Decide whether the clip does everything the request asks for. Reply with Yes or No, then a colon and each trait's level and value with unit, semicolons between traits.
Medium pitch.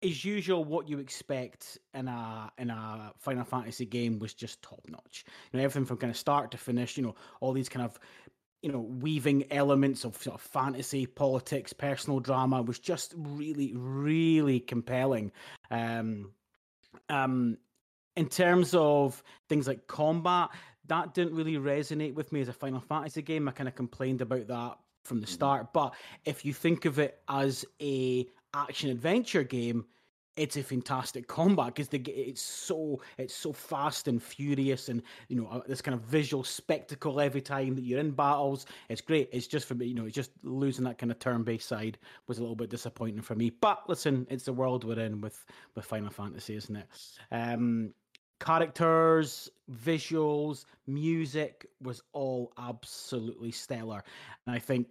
No: low, 130 Hz